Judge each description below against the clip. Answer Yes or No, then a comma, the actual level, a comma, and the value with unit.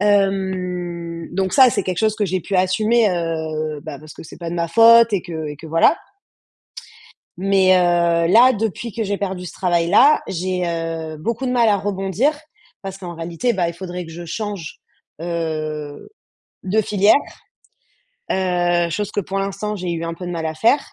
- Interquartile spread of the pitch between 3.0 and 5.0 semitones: Yes, average, 3.4 semitones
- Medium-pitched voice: Yes, medium, 180 Hz